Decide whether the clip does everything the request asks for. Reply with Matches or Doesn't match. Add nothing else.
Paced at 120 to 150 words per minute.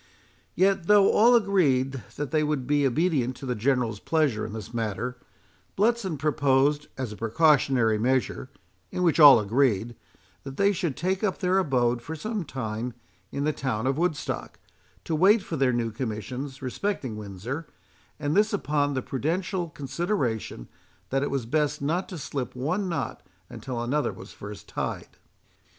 Doesn't match